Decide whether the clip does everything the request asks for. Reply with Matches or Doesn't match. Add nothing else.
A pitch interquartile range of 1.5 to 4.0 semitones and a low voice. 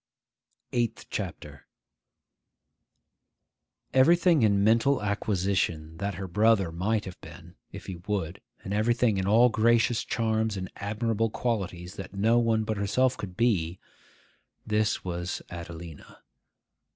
Matches